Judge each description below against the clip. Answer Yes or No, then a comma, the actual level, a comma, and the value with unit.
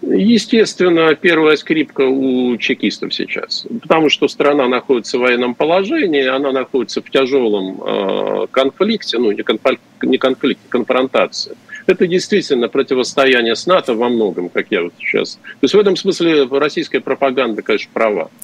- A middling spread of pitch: No, wide, 6.0 semitones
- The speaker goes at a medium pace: Yes, average, 145 wpm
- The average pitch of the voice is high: No, medium, 140 Hz